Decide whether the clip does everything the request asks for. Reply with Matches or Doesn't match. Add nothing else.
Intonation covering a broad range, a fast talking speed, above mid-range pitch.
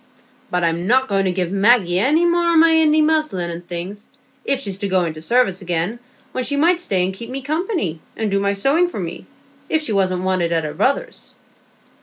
Matches